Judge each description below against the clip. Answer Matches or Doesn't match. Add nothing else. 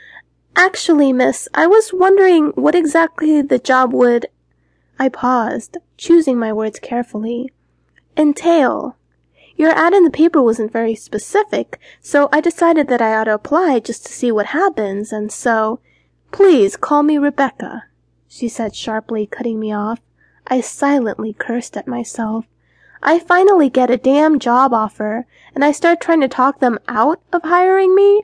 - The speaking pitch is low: Doesn't match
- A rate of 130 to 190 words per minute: Matches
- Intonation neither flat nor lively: Doesn't match